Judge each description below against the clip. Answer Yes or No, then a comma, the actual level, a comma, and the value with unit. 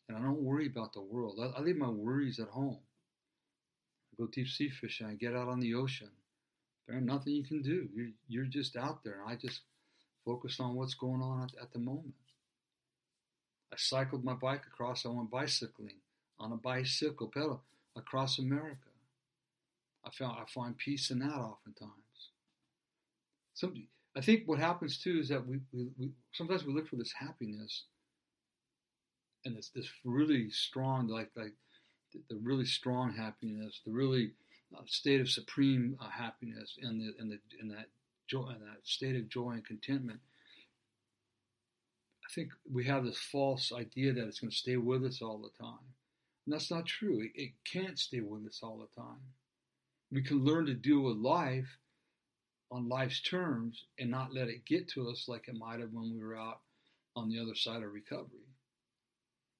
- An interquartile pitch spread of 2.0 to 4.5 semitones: Yes, average, 2.8 semitones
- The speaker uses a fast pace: No, average, 175 wpm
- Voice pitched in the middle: No, low, 125 Hz